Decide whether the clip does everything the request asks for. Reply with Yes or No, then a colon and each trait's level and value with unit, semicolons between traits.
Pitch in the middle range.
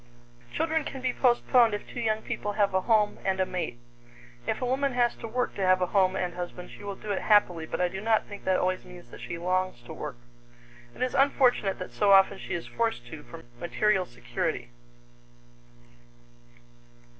No: high, 195 Hz